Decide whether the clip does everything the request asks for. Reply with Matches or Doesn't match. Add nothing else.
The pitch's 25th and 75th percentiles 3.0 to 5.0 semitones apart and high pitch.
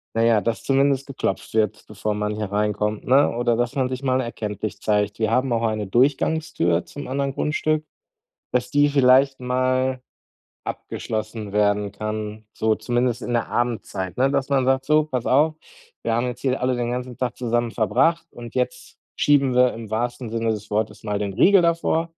Doesn't match